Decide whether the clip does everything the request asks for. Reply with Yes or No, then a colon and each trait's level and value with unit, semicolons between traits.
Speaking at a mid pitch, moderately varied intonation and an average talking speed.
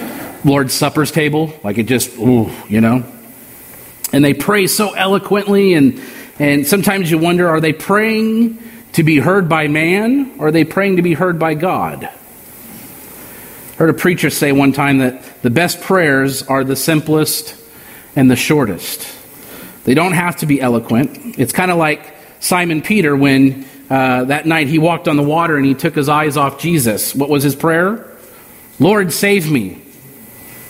Yes: medium, 155 Hz; average, 4.8 semitones; average, 170 wpm